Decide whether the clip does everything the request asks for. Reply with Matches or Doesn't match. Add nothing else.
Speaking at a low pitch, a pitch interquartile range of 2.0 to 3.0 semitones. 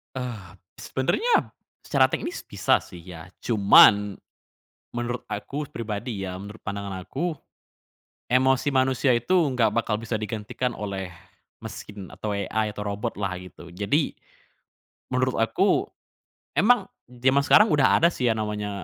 Doesn't match